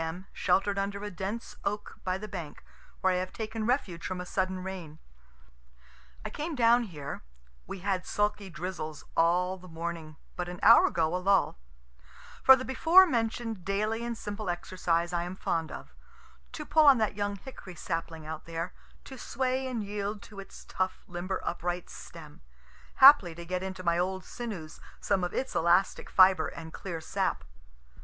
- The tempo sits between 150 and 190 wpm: Yes, average, 175 wpm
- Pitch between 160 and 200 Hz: Yes, high, 190 Hz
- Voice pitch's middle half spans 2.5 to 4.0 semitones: Yes, average, 3.6 semitones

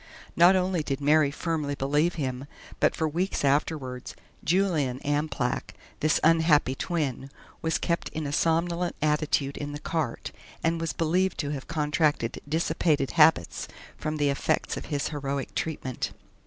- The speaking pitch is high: No, medium, 150 Hz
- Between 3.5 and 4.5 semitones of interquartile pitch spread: No, average, 2.7 semitones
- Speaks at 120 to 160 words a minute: Yes, average, 145 wpm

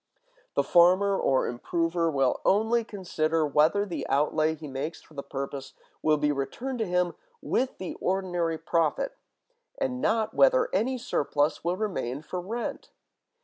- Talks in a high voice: No, medium, 175 Hz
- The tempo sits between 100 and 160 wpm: Yes, average, 145 wpm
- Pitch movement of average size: No, wide, 6.0 semitones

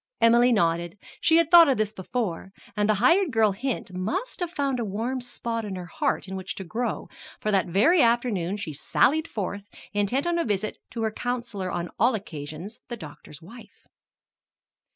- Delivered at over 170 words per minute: Yes, average, 185 wpm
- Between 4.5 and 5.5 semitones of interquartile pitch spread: Yes, average, 4.8 semitones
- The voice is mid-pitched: No, high, 215 Hz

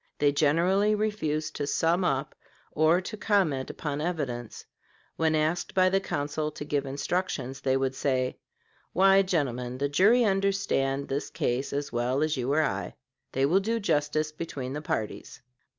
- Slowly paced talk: No, average, 160 wpm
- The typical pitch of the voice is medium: Yes, medium, 150 Hz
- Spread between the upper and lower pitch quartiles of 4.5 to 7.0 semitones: Yes, average, 5.2 semitones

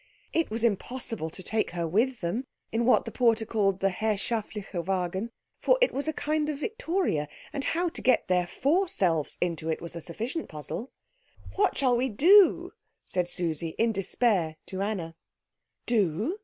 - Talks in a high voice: Yes, high, 220 Hz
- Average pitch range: No, wide, 6.9 semitones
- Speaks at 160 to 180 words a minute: Yes, average, 170 wpm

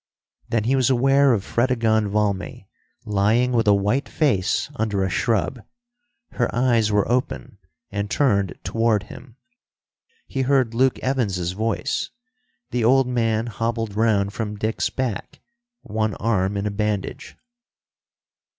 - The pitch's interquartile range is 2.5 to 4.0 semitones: Yes, average, 3.3 semitones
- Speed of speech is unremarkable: No, slow, 130 wpm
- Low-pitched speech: Yes, low, 110 Hz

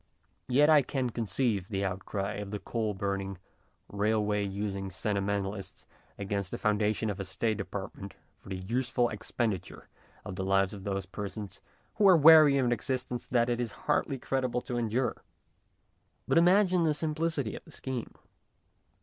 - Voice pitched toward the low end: Yes, low, 110 Hz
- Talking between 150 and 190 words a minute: Yes, average, 160 wpm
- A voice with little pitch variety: No, average, 4.5 semitones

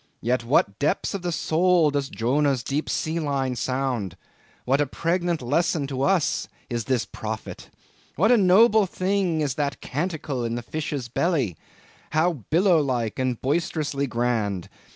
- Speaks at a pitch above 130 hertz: Yes, medium, 140 Hz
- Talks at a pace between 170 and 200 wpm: No, average, 150 wpm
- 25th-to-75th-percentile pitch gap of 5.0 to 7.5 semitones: Yes, wide, 5.4 semitones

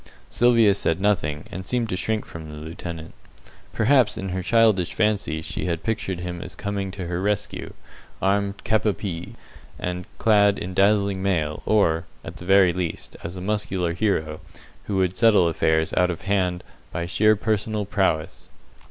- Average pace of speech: Yes, average, 170 wpm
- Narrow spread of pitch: No, average, 3.2 semitones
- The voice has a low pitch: Yes, very low, 95 Hz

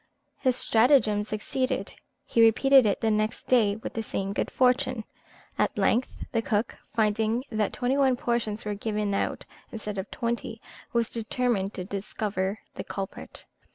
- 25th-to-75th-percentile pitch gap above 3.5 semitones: No, average, 2.8 semitones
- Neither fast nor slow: Yes, average, 155 wpm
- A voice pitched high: Yes, high, 220 Hz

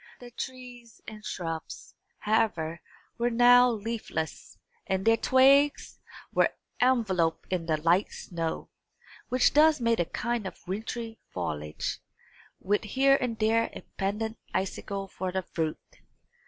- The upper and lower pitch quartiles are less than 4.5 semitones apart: No, average, 5.0 semitones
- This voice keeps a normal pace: No, slow, 125 wpm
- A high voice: Yes, high, 220 Hz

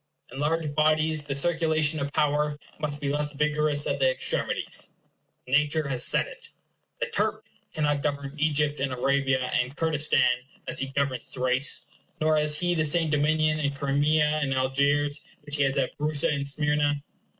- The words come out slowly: No, average, 165 wpm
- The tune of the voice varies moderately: No, narrow, 1.6 semitones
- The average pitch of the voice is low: No, medium, 145 Hz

